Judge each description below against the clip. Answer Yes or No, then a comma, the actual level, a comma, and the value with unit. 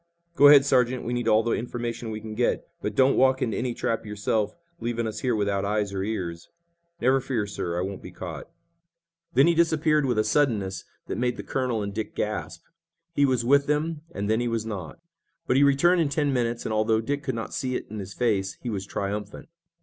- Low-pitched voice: Yes, low, 115 Hz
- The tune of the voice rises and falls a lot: No, average, 4.1 semitones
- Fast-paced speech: Yes, fast, 220 wpm